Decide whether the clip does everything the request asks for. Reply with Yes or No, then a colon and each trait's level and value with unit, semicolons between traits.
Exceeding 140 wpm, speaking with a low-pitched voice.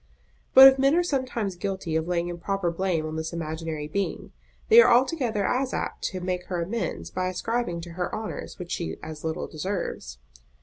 No: average, 185 wpm; medium, 185 Hz